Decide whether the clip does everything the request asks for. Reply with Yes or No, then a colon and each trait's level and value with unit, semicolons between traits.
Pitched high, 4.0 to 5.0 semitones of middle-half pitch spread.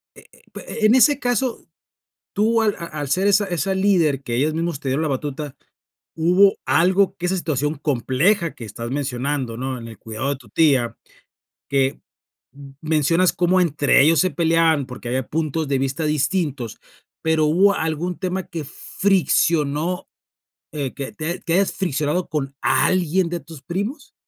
No: medium, 160 Hz; average, 4.7 semitones